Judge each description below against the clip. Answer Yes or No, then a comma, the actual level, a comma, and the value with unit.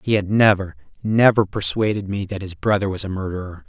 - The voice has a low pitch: Yes, low, 100 Hz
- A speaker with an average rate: Yes, average, 195 wpm